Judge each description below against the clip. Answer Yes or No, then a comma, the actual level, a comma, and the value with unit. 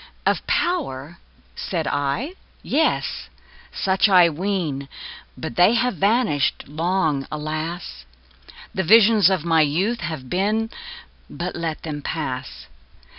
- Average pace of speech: No, slow, 115 wpm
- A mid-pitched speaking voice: Yes, medium, 170 Hz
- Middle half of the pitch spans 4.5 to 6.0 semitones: Yes, average, 5.1 semitones